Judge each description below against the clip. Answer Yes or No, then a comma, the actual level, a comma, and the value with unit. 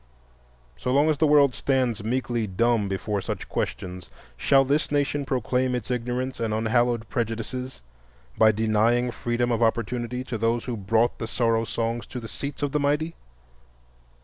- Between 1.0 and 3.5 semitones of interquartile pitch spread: Yes, narrow, 2.5 semitones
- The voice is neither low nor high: No, low, 120 Hz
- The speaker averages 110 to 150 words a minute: No, average, 160 wpm